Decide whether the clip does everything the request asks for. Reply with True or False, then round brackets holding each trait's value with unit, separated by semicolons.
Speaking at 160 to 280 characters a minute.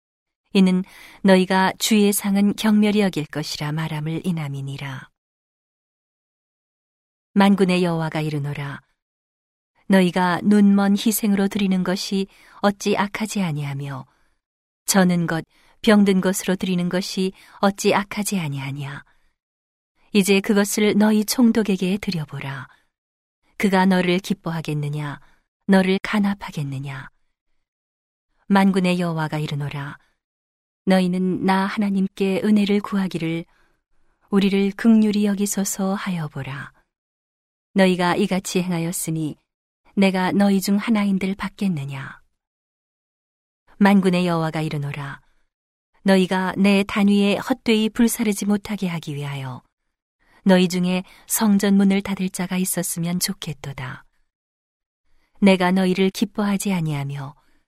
True (255 characters per minute)